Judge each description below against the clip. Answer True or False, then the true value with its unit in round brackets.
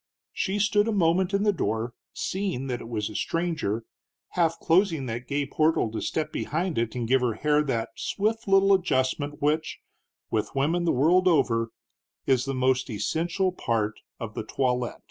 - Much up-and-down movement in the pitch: True (6.5 semitones)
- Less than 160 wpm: False (175 wpm)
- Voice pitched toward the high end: False (145 Hz)